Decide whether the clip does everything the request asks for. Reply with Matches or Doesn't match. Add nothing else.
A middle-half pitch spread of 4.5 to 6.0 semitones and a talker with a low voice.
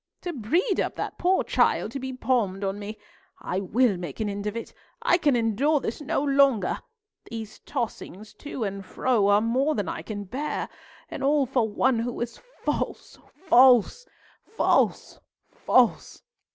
Doesn't match